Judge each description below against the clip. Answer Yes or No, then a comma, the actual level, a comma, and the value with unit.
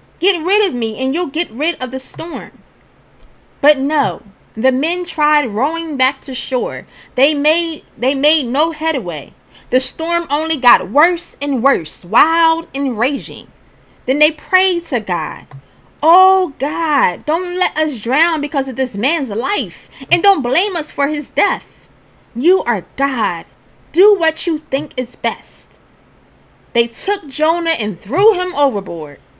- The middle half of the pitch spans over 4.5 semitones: No, average, 4.2 semitones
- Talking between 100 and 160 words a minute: Yes, average, 155 wpm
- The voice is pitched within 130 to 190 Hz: No, very high, 300 Hz